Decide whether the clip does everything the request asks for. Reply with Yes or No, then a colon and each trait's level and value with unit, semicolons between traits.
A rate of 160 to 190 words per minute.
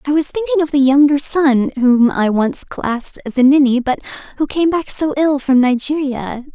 No: average, 200 wpm